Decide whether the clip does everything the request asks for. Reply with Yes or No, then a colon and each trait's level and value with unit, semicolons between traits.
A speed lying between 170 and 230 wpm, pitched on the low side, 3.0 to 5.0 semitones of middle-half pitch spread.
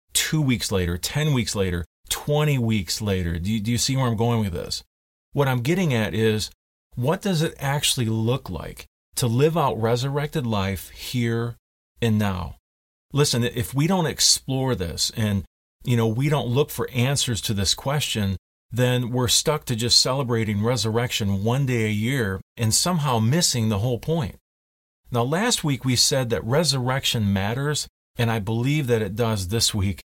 No: average, 175 wpm; low, 115 Hz; wide, 5.5 semitones